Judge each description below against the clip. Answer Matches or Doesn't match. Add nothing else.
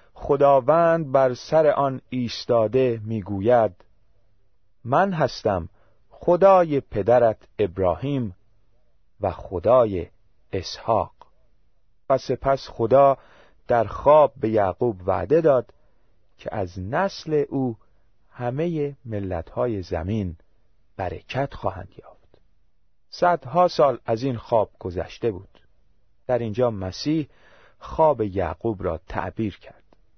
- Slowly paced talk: Matches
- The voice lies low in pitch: Matches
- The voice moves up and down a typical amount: Doesn't match